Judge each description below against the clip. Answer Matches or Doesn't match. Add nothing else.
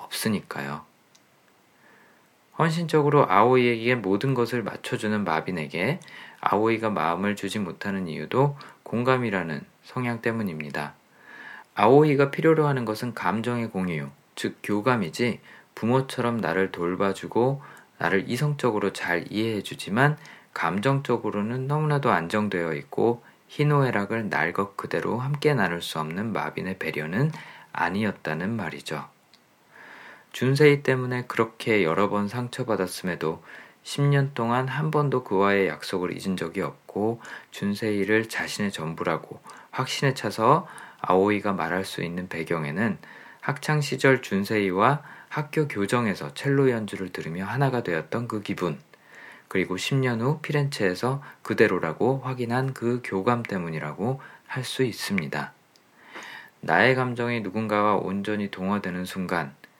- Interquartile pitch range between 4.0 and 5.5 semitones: Matches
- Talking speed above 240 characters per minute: Matches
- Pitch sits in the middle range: Doesn't match